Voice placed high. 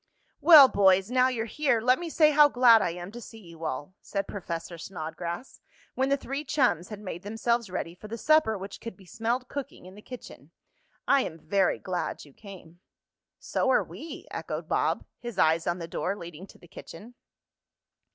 Yes: high, 205 Hz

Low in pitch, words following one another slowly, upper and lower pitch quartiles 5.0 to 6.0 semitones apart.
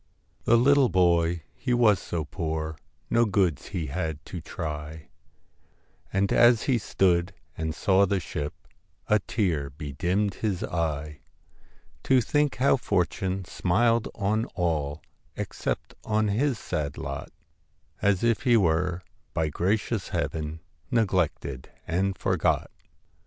Yes: very low, 90 Hz; slow, 125 wpm; average, 5.3 semitones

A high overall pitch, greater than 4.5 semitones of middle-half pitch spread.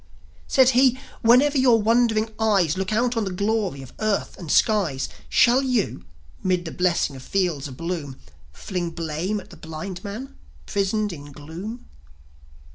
Yes: high, 195 Hz; average, 5.2 semitones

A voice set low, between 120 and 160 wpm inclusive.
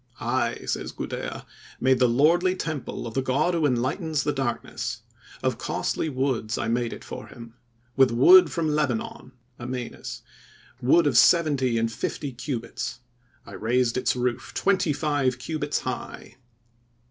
Yes: low, 130 Hz; average, 145 wpm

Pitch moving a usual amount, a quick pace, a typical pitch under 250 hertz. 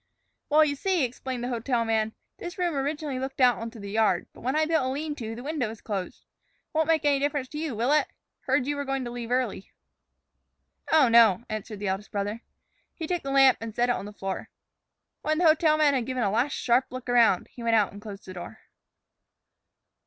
No: average, 4.5 semitones; fast, 225 wpm; very high, 255 Hz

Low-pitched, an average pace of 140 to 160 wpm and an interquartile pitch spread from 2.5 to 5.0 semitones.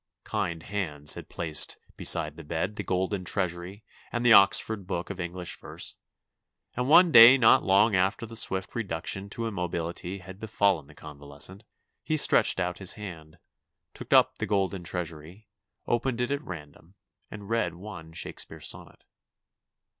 Yes: very low, 95 Hz; average, 155 wpm; average, 4.1 semitones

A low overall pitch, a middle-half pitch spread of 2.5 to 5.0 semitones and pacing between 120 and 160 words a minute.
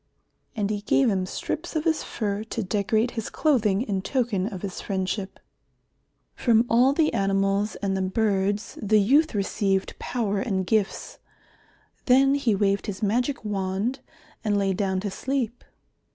No: high, 210 Hz; average, 3.6 semitones; average, 150 wpm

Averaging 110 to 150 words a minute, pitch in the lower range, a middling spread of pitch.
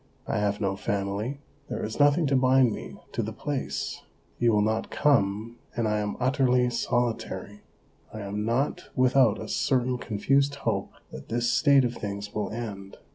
No: average, 170 wpm; low, 115 Hz; average, 3.8 semitones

